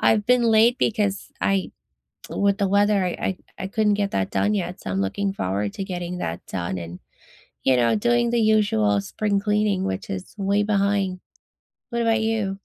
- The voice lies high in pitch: Yes, high, 200 Hz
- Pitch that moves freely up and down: No, average, 3.7 semitones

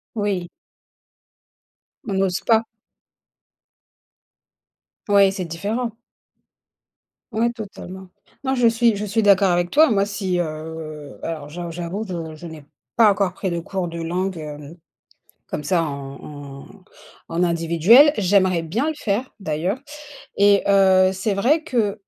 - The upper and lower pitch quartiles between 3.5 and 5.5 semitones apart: Yes, average, 3.8 semitones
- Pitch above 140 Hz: Yes, high, 190 Hz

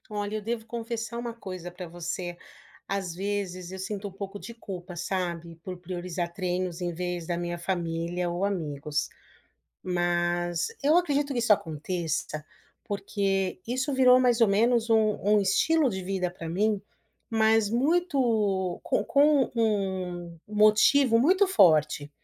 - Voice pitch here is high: Yes, high, 195 Hz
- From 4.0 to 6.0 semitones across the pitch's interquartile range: Yes, average, 4.5 semitones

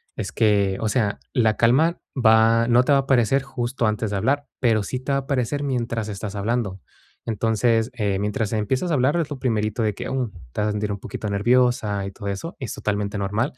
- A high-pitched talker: No, low, 115 Hz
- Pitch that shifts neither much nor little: Yes, average, 3.6 semitones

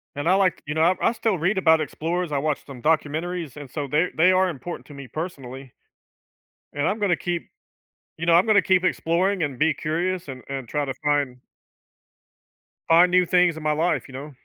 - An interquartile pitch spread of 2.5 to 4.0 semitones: Yes, average, 3.7 semitones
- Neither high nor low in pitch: Yes, medium, 160 Hz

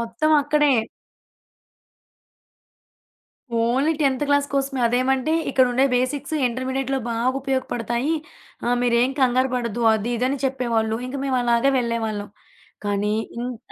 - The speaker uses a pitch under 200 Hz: No, very high, 250 Hz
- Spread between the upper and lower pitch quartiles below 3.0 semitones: Yes, narrow, 2.4 semitones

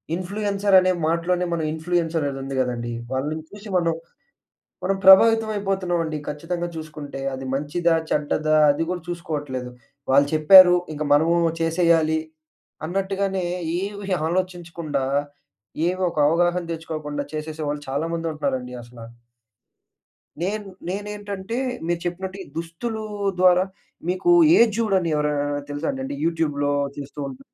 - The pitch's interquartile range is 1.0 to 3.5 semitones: No, average, 4.0 semitones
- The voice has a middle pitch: Yes, medium, 170 Hz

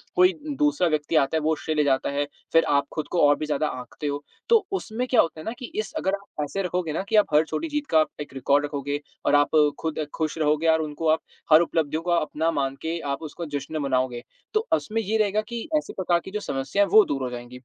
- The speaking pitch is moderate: Yes, medium, 155 Hz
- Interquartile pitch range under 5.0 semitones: No, average, 5.3 semitones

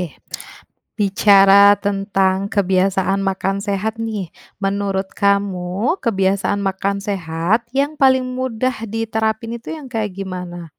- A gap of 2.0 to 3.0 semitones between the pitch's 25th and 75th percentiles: Yes, average, 2.7 semitones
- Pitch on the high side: Yes, high, 200 Hz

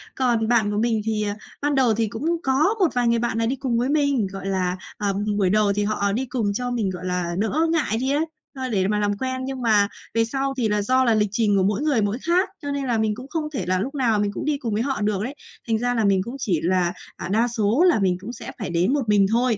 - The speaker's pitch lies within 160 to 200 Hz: No, high, 225 Hz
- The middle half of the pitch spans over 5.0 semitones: No, average, 4.3 semitones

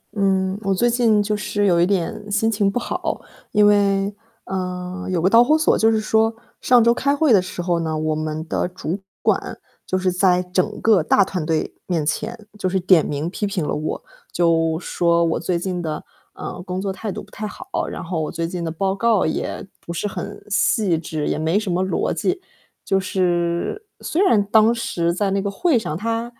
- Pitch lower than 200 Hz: Yes, high, 190 Hz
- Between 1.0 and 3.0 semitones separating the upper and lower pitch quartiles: No, average, 3.5 semitones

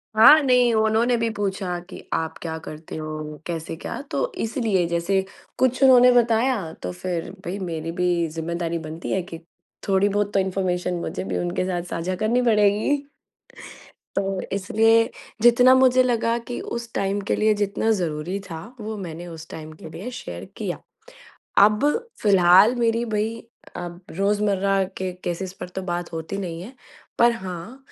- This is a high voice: Yes, high, 195 Hz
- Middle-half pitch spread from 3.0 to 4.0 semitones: No, average, 4.8 semitones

